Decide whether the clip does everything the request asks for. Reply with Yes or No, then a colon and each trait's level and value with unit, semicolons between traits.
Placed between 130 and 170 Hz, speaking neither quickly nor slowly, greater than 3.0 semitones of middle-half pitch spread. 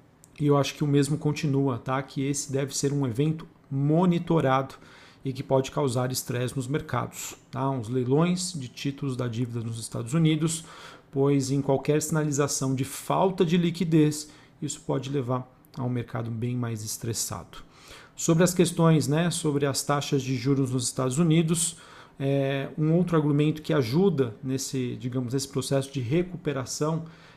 No: medium, 140 Hz; average, 160 wpm; average, 2.7 semitones